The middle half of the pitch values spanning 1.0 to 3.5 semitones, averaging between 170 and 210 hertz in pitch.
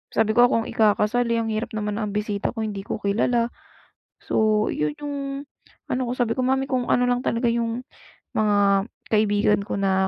No: average, 2.8 semitones; high, 220 Hz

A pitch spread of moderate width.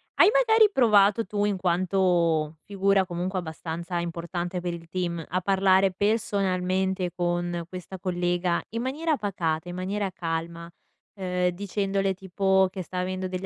No: narrow, 2.0 semitones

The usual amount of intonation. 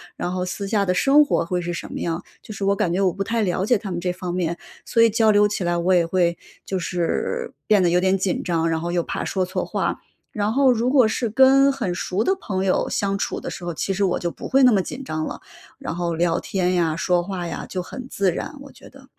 Yes: average, 3.8 semitones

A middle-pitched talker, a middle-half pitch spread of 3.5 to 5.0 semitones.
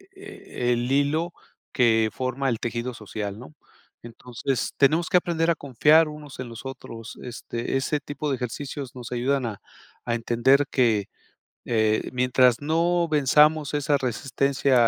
No: low, 130 Hz; average, 3.8 semitones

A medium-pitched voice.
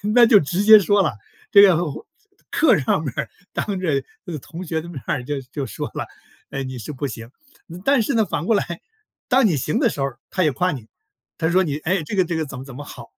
Yes: medium, 165 Hz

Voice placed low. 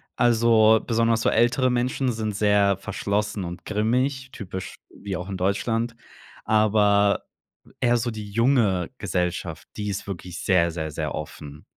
Yes: low, 105 Hz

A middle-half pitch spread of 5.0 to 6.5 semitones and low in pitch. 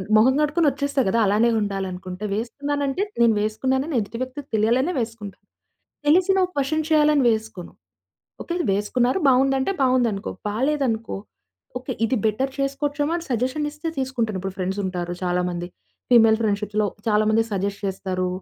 No: wide, 5.4 semitones; high, 235 Hz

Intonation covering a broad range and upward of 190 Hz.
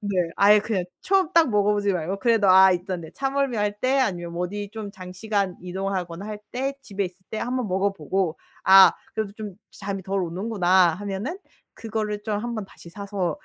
No: average, 2.7 semitones; high, 200 Hz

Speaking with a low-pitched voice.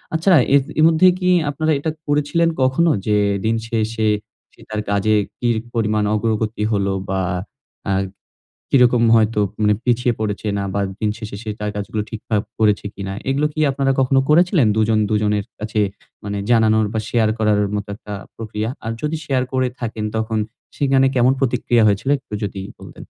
Yes: low, 110 Hz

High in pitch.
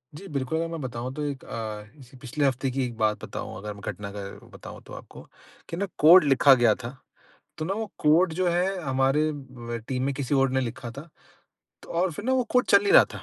No: medium, 140 Hz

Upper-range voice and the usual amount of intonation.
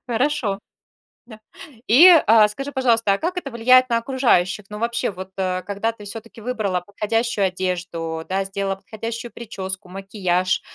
Yes: high, 210 Hz; average, 3.7 semitones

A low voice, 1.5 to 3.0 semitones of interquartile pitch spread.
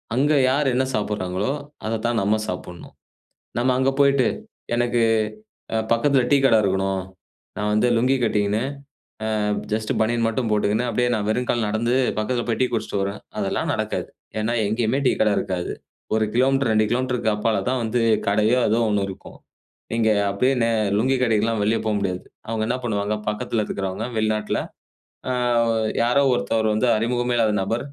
Yes: low, 110 Hz; average, 2.7 semitones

